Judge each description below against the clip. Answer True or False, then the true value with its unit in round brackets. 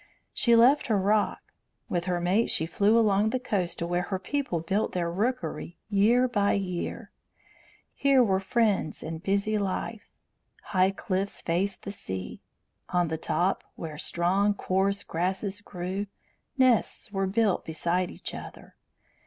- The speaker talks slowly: False (145 wpm)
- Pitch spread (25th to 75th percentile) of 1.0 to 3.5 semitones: True (3.2 semitones)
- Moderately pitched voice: False (195 Hz)